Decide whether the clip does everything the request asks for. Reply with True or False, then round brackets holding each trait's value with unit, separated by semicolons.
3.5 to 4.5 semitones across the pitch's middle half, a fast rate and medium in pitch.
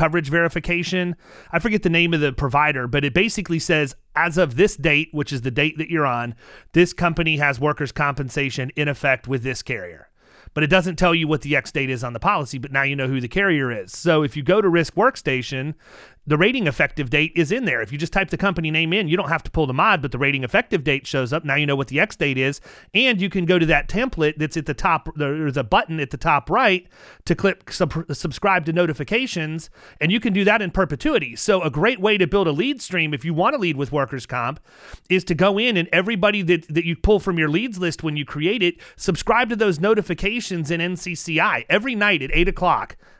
True (4.2 semitones; 245 wpm; 165 Hz)